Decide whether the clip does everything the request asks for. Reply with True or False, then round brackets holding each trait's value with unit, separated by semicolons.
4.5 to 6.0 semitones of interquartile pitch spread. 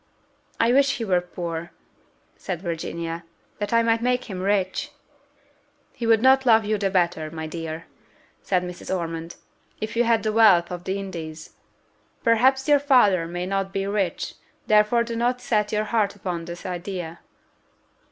True (4.9 semitones)